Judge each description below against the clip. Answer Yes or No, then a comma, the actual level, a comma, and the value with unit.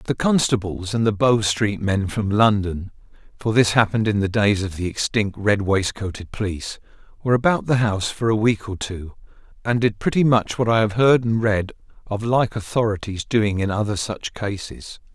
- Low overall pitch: Yes, low, 105 Hz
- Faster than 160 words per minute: Yes, average, 180 wpm